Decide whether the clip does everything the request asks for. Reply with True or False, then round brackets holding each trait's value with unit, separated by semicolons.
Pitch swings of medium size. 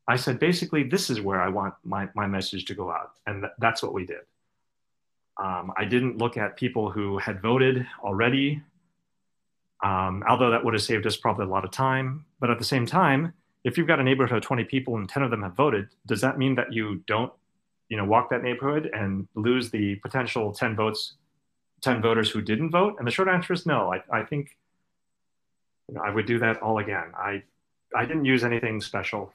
True (4.4 semitones)